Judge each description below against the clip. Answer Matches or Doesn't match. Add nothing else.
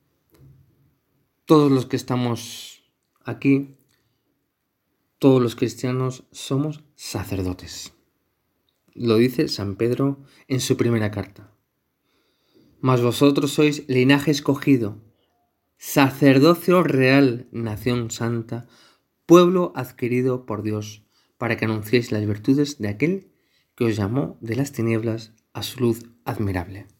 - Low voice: Matches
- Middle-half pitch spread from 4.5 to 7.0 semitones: Doesn't match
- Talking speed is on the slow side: Matches